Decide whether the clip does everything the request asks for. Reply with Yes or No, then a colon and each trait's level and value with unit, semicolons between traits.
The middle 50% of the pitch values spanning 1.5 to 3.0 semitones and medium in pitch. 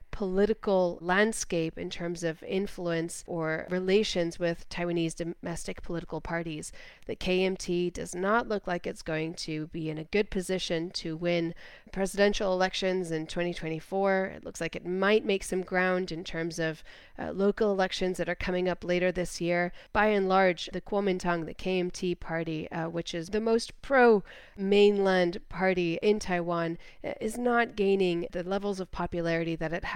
Yes: narrow, 2.5 semitones; medium, 180 Hz